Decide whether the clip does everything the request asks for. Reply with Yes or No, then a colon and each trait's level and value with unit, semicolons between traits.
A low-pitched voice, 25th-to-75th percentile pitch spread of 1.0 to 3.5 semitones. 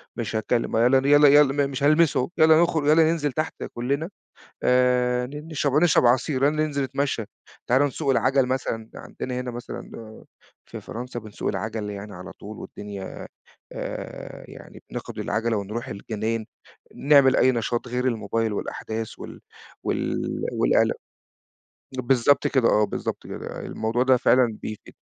No: low, 125 Hz; average, 4.0 semitones